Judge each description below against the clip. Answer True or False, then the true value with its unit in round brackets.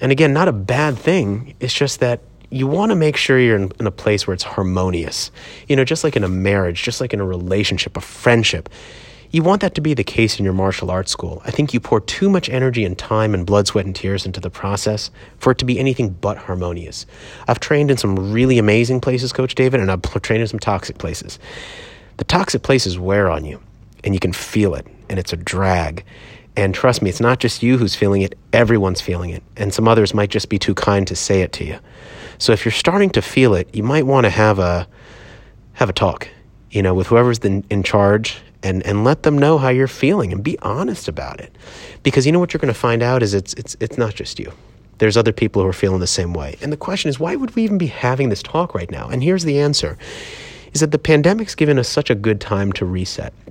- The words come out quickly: True (245 wpm)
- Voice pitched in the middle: False (110 Hz)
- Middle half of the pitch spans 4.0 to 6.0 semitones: True (5.1 semitones)